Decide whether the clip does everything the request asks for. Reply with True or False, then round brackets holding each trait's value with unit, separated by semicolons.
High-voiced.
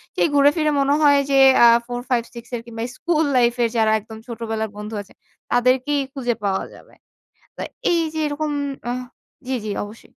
True (245 Hz)